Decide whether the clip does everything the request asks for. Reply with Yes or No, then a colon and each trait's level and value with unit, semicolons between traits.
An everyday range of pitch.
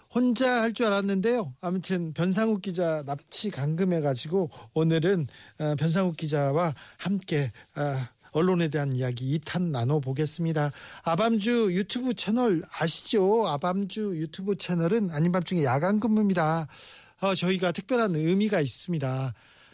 Yes: average, 4.8 semitones